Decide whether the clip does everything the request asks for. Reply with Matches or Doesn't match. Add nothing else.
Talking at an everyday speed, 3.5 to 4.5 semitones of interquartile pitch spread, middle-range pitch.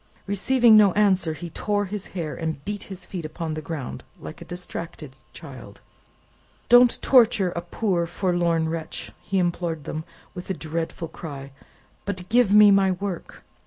Matches